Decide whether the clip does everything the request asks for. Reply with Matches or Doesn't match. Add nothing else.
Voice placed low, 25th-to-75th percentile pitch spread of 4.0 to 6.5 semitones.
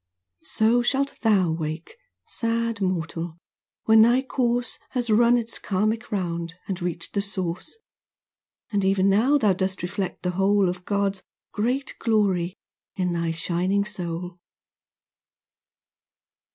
Doesn't match